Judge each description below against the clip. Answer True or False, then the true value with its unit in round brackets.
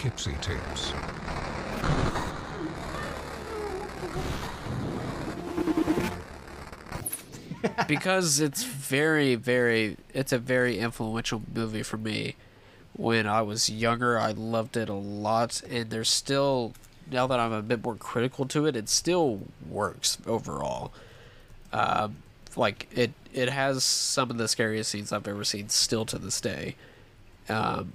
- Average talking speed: False (115 wpm)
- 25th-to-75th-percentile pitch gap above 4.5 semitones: False (3.3 semitones)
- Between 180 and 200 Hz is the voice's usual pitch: False (115 Hz)